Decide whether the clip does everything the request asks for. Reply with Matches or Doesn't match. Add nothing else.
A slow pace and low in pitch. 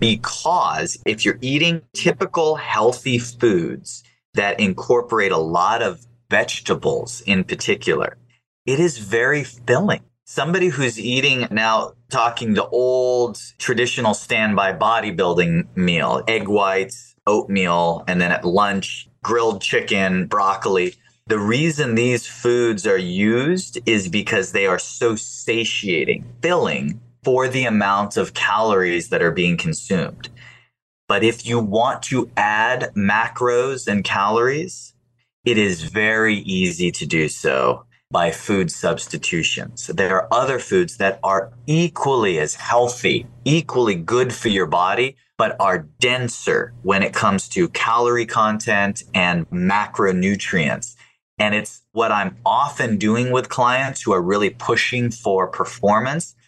Matches